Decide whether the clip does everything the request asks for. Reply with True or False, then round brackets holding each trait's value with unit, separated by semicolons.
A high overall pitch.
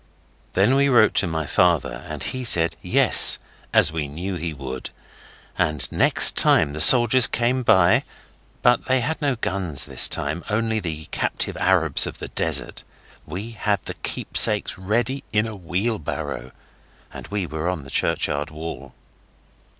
False (90 Hz)